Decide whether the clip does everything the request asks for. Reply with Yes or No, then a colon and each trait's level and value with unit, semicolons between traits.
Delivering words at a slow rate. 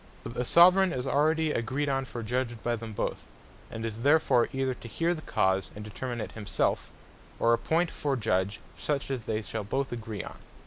No: average, 195 wpm